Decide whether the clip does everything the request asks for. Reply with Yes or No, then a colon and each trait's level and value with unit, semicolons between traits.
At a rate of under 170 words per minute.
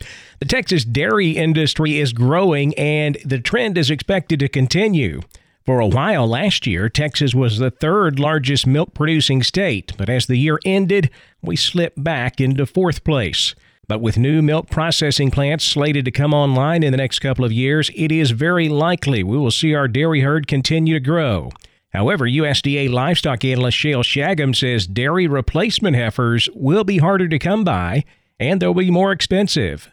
No: average, 175 wpm